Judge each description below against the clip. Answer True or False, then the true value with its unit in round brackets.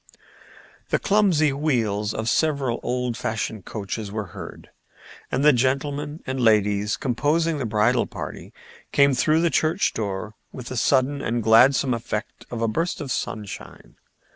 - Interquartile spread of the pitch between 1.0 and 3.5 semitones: False (4.8 semitones)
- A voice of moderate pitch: False (125 Hz)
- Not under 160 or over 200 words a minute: False (145 wpm)